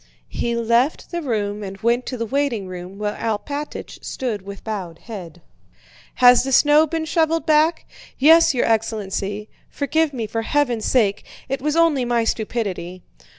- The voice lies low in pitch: No, high, 235 Hz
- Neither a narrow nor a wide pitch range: No, wide, 5.7 semitones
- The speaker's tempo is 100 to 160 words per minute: Yes, average, 155 wpm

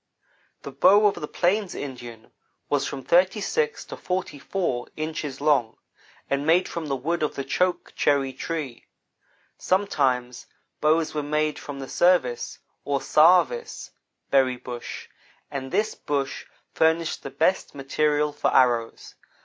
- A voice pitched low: No, medium, 150 Hz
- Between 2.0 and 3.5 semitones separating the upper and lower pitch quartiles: No, average, 4.4 semitones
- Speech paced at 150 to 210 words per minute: No, average, 140 wpm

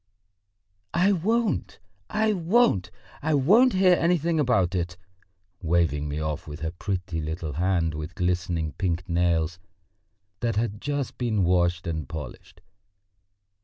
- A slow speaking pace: Yes, slow, 130 wpm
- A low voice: Yes, very low, 90 Hz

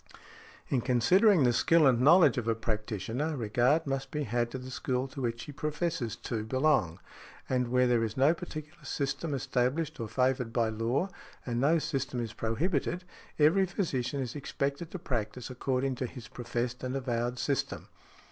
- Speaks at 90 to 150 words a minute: No, average, 175 wpm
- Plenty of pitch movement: No, average, 3.9 semitones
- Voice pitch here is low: Yes, low, 130 Hz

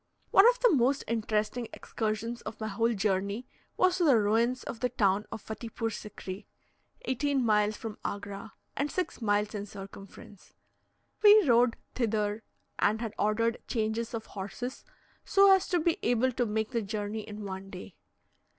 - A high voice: Yes, high, 220 Hz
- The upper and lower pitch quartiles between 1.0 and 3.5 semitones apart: Yes, average, 3.1 semitones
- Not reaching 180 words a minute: Yes, average, 160 wpm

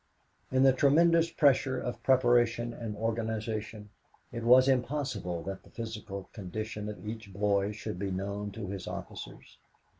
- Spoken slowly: No, average, 145 wpm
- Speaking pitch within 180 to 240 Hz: No, low, 110 Hz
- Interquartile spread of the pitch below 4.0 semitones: Yes, average, 3.6 semitones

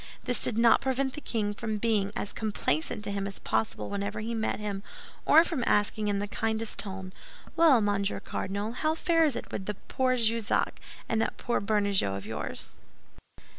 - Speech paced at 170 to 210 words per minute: Yes, average, 180 wpm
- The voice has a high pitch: Yes, high, 215 Hz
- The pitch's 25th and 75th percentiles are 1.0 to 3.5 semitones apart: Yes, average, 2.8 semitones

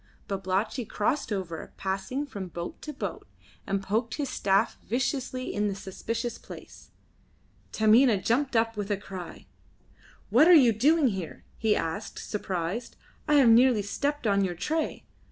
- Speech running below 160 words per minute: Yes, average, 150 wpm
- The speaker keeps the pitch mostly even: No, average, 4.8 semitones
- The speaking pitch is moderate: No, high, 220 Hz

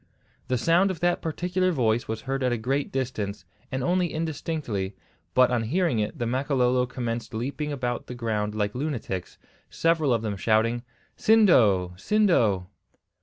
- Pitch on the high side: No, low, 125 Hz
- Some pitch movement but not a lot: No, wide, 6.0 semitones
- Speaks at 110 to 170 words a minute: Yes, average, 155 wpm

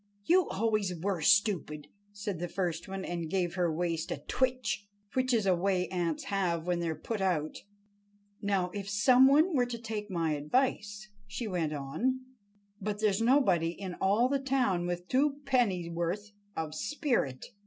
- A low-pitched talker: No, high, 195 Hz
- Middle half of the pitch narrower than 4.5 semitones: No, average, 4.8 semitones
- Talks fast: No, average, 165 wpm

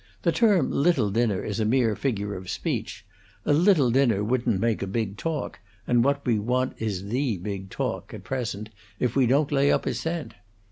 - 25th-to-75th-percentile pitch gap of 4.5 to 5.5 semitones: Yes, average, 4.9 semitones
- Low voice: Yes, low, 120 Hz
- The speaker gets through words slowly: No, average, 195 wpm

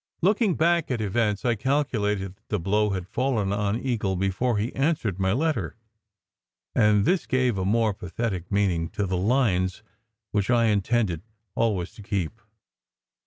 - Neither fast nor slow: Yes, average, 155 wpm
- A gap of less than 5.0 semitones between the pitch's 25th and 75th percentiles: Yes, average, 3.9 semitones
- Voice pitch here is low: Yes, low, 105 Hz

